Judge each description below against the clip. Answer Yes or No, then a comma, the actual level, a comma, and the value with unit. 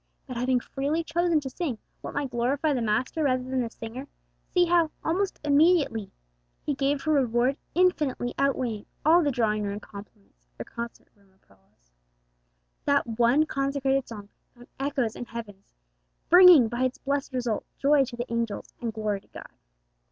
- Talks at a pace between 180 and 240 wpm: No, average, 165 wpm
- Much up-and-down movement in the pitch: No, average, 3.9 semitones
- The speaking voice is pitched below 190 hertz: No, very high, 255 Hz